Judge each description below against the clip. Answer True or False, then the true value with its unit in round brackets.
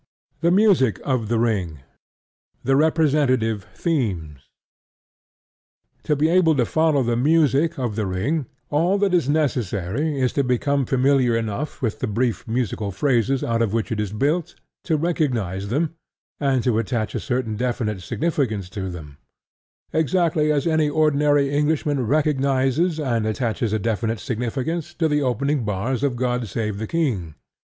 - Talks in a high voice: False (130 Hz)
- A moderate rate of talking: True (150 wpm)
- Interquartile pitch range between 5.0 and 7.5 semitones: True (5.4 semitones)